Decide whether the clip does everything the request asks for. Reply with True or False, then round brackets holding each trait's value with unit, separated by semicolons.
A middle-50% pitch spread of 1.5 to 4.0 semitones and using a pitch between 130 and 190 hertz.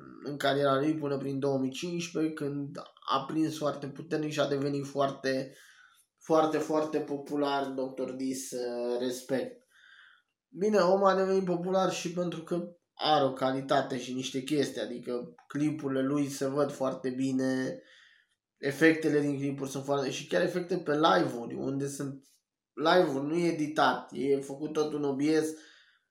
True (2.6 semitones; 140 Hz)